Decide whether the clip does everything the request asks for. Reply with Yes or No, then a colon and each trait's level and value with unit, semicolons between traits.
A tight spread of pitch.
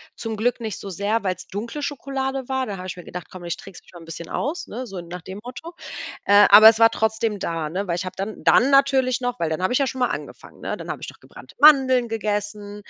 No: average, 5.3 semitones